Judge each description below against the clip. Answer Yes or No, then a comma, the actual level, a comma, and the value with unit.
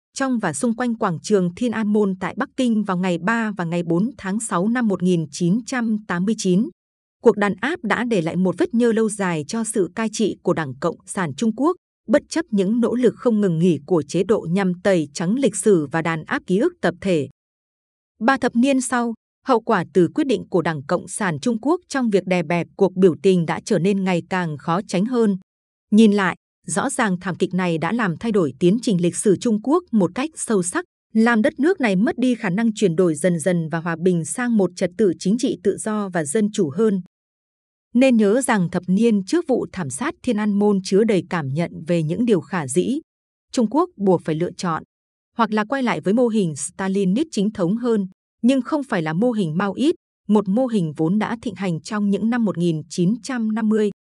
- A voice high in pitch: Yes, high, 205 Hz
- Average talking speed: Yes, average, 225 wpm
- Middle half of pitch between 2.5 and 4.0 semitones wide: No, average, 4.5 semitones